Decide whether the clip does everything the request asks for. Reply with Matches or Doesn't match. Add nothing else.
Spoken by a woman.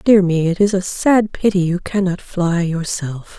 Matches